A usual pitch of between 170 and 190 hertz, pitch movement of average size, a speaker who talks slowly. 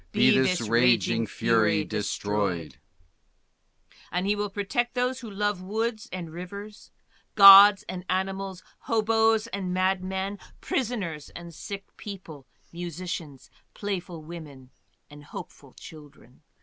No: medium, 185 Hz; wide, 5.9 semitones; slow, 110 wpm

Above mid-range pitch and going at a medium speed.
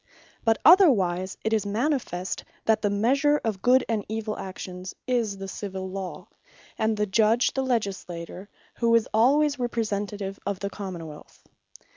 Yes: high, 210 Hz; average, 150 wpm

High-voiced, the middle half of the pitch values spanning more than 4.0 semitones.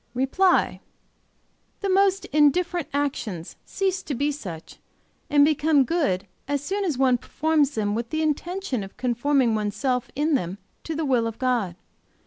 Yes: very high, 280 Hz; average, 5.2 semitones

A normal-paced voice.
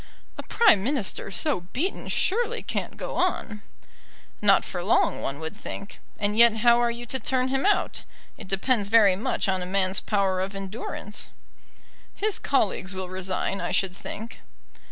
Yes: average, 165 wpm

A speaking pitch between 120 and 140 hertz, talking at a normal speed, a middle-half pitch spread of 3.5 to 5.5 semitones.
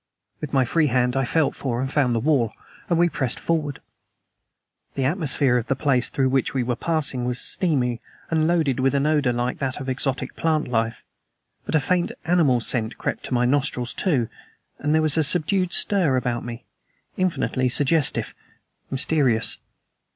Yes: low, 135 Hz; average, 175 wpm; average, 4.0 semitones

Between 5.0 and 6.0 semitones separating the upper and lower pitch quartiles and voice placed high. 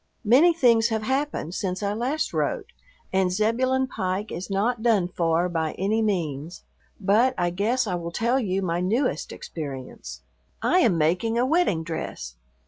Yes: wide, 5.5 semitones; high, 200 Hz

